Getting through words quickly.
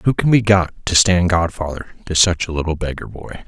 Yes: fast, 225 wpm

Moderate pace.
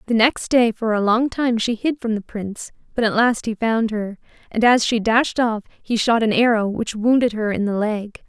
No: fast, 240 wpm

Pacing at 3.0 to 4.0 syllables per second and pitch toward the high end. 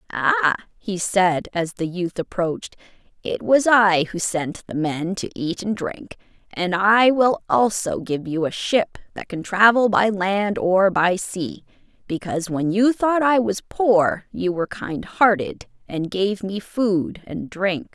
Yes: 3.8 syllables/s; high, 195 Hz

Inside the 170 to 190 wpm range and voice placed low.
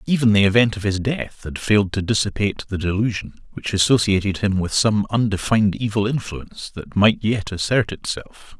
Yes: average, 175 wpm; low, 105 Hz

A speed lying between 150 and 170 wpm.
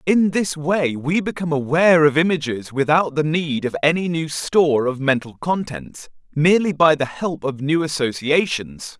Yes: average, 165 wpm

